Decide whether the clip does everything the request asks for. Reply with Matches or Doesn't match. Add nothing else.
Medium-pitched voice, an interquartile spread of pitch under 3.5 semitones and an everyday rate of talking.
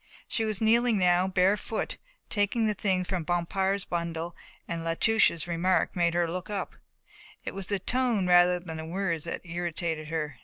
Matches